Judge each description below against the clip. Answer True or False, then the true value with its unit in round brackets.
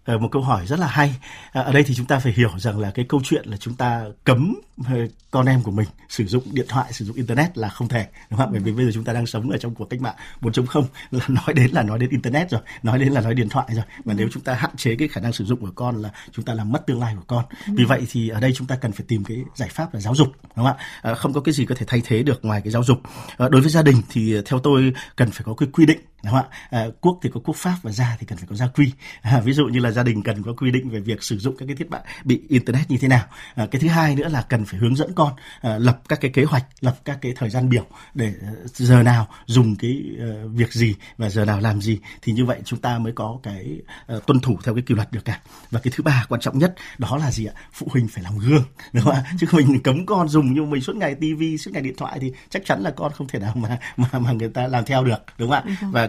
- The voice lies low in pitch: True (125 Hz)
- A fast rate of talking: True (300 wpm)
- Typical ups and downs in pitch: True (3.3 semitones)